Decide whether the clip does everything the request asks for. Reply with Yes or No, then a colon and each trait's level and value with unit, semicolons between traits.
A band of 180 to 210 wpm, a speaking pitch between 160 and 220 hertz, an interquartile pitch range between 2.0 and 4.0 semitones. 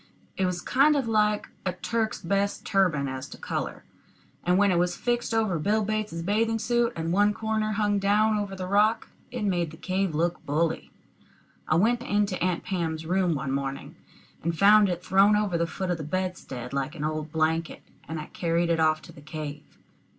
No: average, 195 wpm; medium, 185 Hz; average, 4.4 semitones